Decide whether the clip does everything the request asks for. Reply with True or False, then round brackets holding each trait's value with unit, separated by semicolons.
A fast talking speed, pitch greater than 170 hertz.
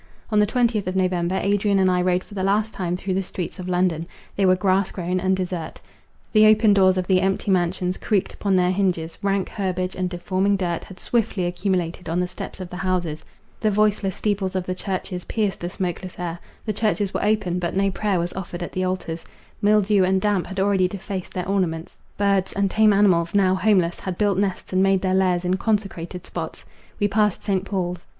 True (210 wpm; 185 Hz)